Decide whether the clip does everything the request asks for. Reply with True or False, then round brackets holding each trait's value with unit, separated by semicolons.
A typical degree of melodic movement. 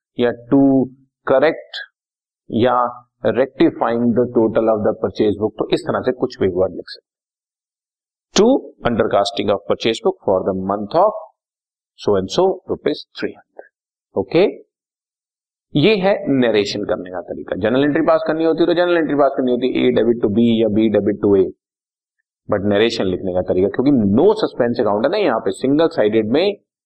True (4.7 semitones)